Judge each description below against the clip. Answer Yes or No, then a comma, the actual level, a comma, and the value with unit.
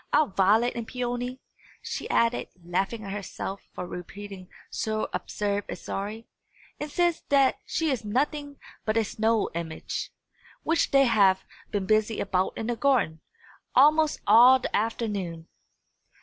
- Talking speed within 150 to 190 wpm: No, slow, 135 wpm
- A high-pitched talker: Yes, high, 220 Hz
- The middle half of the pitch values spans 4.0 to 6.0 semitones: Yes, average, 4.5 semitones